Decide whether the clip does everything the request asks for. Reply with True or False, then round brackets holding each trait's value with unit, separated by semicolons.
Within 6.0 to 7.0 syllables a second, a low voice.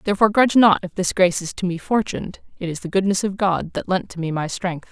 False (6.5 syllables/s; 185 Hz)